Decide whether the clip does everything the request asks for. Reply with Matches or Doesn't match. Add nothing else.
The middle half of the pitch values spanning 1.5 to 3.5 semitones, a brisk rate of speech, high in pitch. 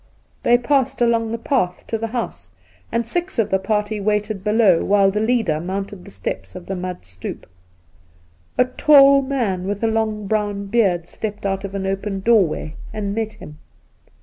Doesn't match